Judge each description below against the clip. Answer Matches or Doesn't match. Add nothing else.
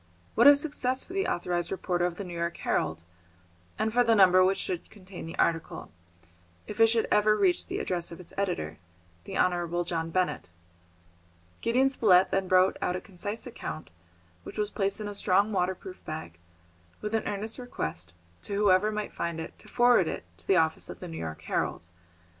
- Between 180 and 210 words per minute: Matches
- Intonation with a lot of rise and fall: Doesn't match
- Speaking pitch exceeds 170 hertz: Matches